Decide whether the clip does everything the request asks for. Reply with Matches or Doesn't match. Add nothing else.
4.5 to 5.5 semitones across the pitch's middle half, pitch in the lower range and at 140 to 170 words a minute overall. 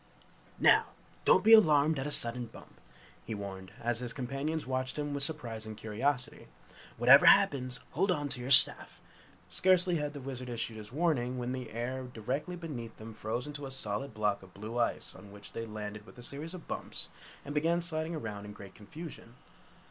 Doesn't match